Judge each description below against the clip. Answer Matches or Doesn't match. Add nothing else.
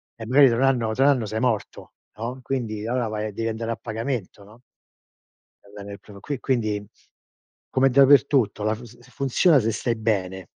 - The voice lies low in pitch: Matches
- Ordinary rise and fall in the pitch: Matches